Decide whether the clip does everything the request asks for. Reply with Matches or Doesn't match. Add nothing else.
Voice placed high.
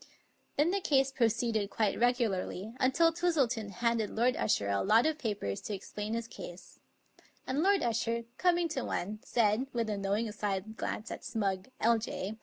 Matches